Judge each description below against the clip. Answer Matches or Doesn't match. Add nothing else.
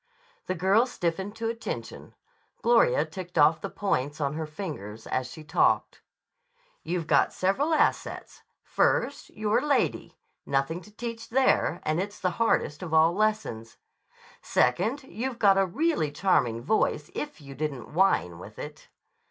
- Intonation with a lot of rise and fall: Matches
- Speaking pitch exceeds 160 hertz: Matches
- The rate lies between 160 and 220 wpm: Doesn't match